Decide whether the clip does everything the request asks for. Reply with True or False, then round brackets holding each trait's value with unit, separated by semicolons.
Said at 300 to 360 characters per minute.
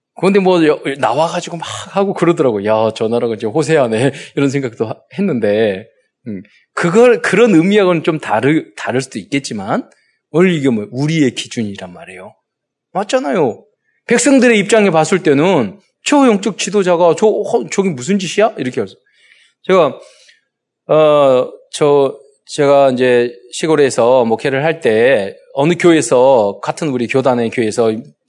True (305 characters per minute)